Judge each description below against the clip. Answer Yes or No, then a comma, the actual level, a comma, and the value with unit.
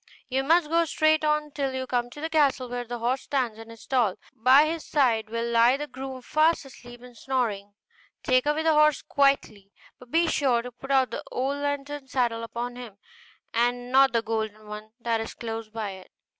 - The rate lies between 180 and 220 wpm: Yes, average, 200 wpm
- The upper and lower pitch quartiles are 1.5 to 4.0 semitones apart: Yes, average, 3.6 semitones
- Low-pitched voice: No, very high, 250 Hz